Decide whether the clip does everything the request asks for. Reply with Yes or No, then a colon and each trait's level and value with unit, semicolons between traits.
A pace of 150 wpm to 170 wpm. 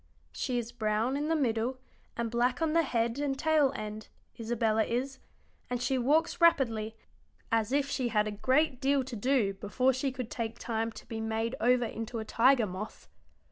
No: average, 185 wpm